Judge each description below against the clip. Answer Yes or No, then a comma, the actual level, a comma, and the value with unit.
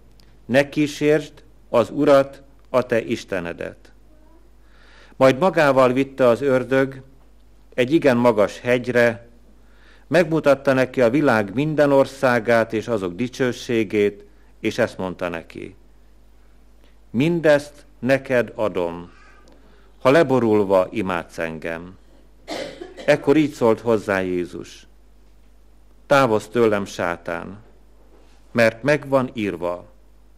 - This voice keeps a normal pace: No, slow, 95 wpm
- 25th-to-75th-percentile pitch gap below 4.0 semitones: No, average, 5.1 semitones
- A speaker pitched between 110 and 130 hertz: Yes, low, 120 Hz